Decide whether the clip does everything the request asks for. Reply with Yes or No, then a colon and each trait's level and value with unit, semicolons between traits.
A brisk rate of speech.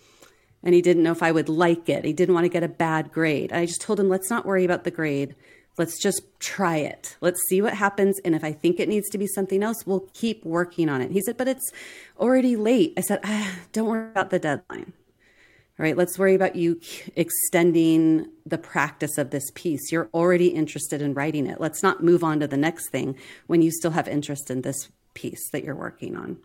Yes: fast, 230 wpm